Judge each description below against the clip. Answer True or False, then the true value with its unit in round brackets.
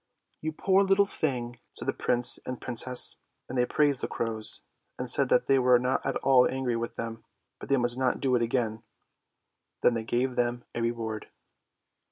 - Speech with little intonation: True (2.0 semitones)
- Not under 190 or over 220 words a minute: True (200 wpm)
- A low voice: True (125 Hz)